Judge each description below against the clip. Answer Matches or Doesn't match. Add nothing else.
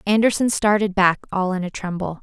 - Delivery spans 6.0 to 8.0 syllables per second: Doesn't match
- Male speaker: Doesn't match